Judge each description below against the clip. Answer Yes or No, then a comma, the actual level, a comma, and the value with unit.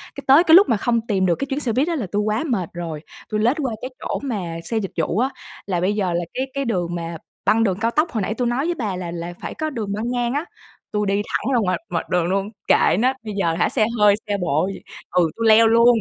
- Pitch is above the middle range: Yes, high, 215 Hz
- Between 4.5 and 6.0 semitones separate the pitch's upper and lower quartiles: Yes, average, 5.1 semitones